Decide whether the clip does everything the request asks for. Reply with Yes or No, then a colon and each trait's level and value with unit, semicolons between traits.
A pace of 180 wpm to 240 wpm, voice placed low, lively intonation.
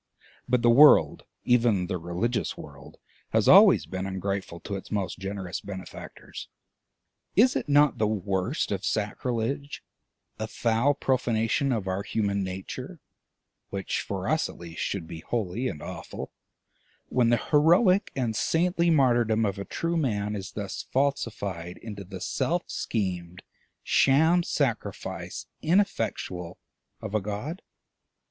No: slow, 135 wpm; low, 110 Hz; wide, 5.8 semitones